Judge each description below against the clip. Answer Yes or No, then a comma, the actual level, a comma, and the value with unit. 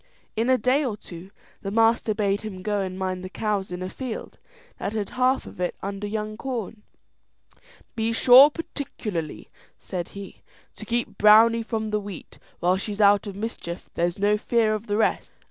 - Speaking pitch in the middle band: No, high, 210 Hz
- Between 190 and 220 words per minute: No, average, 180 wpm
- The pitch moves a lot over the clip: No, average, 2.8 semitones